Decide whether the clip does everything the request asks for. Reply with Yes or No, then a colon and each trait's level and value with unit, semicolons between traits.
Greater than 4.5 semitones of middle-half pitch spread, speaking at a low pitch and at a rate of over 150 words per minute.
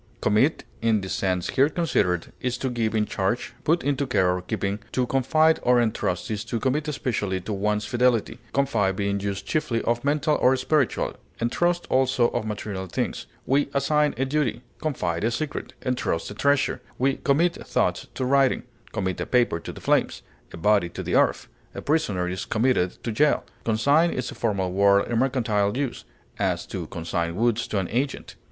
Yes: wide, 5.4 semitones; low, 120 Hz; average, 185 wpm